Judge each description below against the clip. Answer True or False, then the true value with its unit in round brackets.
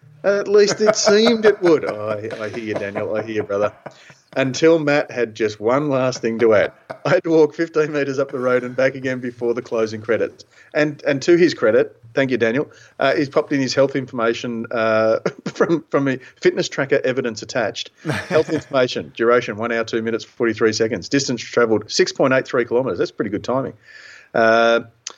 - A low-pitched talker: True (130 Hz)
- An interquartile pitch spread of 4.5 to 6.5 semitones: True (5.2 semitones)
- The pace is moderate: True (195 wpm)